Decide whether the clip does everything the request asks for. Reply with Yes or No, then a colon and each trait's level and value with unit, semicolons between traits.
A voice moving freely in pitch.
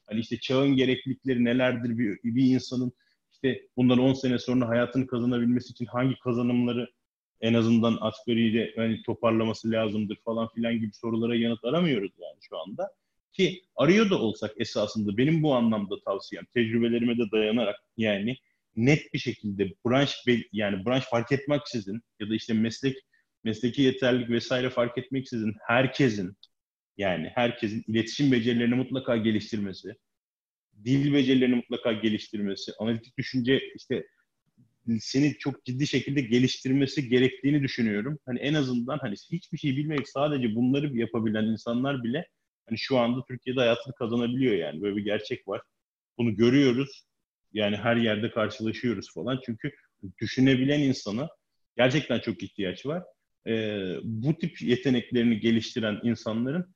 No: narrow, 2.6 semitones